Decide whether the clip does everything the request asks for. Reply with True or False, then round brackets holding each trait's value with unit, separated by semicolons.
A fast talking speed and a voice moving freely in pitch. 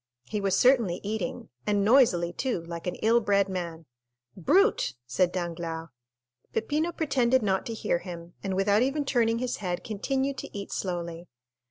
False (160 wpm; 5.8 semitones)